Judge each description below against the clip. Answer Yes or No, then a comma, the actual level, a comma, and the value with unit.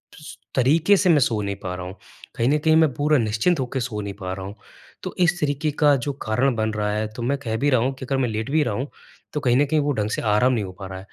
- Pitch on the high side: No, low, 125 Hz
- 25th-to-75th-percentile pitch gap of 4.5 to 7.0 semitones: Yes, wide, 5.4 semitones